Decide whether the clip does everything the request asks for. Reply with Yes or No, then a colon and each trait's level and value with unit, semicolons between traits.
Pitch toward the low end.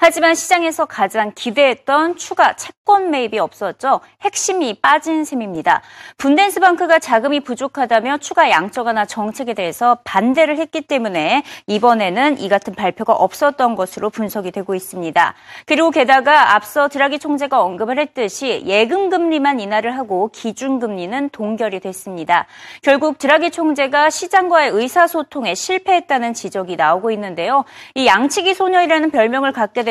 No: very high, 270 Hz